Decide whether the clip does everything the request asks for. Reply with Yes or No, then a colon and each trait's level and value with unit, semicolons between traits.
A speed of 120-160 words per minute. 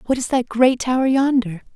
No: fast, 205 wpm